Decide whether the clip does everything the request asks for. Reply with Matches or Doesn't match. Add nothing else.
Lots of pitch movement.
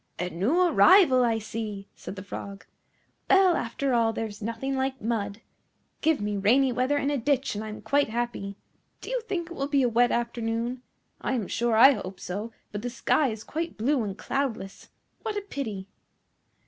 Doesn't match